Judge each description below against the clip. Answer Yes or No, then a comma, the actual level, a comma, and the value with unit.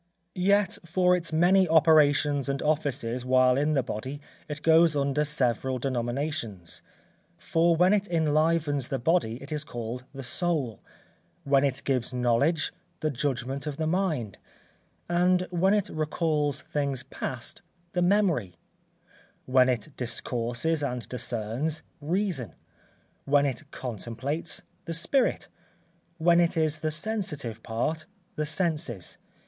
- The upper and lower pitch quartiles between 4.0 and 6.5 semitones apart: Yes, average, 4.6 semitones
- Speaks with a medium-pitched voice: Yes, medium, 145 Hz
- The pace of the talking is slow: Yes, slow, 130 wpm